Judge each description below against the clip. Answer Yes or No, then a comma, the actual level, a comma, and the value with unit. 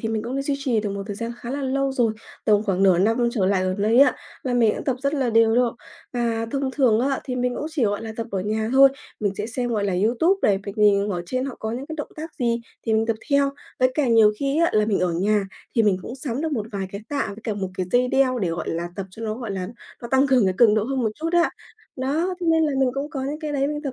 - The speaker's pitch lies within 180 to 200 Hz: No, high, 235 Hz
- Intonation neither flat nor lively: Yes, average, 4.6 semitones